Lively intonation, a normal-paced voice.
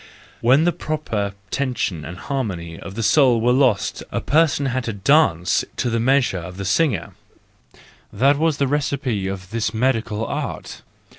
Yes: wide, 5.9 semitones; average, 155 wpm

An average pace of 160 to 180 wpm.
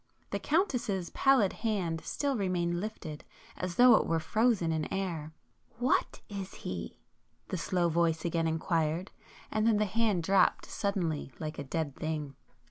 No: average, 145 wpm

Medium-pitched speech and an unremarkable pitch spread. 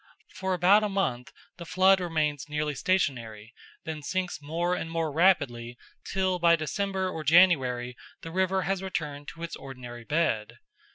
Yes: medium, 165 Hz; average, 5.0 semitones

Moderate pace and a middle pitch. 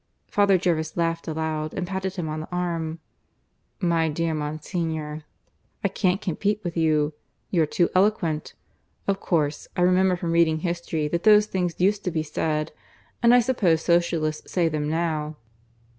Yes: average, 160 wpm; medium, 170 Hz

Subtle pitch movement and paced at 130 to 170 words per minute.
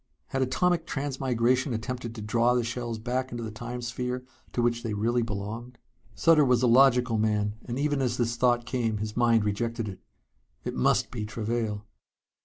No: narrow, 2.2 semitones; average, 180 wpm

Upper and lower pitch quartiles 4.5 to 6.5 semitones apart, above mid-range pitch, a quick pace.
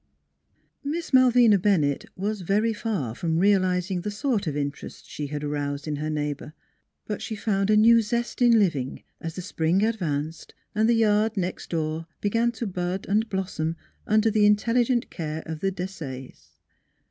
No: wide, 5.5 semitones; high, 195 Hz; average, 170 wpm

